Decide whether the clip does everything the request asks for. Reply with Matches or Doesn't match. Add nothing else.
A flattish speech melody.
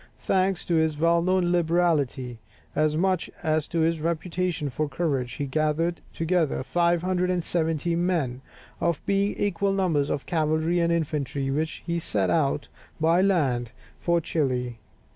Doesn't match